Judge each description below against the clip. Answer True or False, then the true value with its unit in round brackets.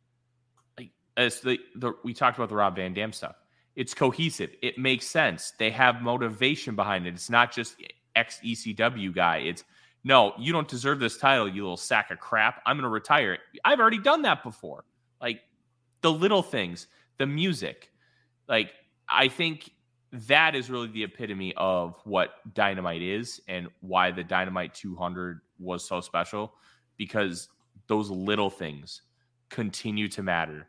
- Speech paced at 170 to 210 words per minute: False (155 wpm)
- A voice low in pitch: True (115 Hz)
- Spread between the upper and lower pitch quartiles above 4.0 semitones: True (5.0 semitones)